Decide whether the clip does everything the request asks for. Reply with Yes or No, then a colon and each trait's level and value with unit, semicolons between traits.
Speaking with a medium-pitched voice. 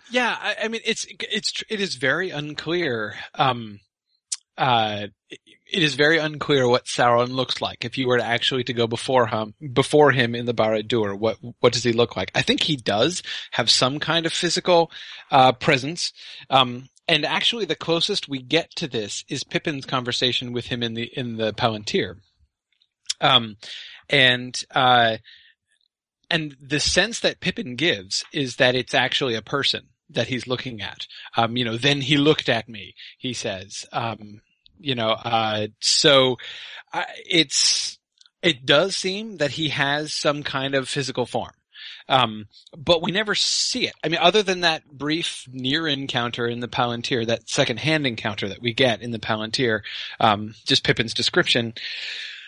No: low, 130 Hz